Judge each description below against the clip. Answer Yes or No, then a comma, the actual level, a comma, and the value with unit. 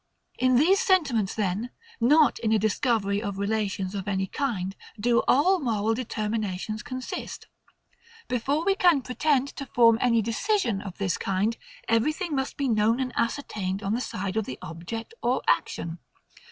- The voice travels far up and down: No, average, 4.8 semitones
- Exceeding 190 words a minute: No, average, 155 wpm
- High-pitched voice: Yes, high, 230 Hz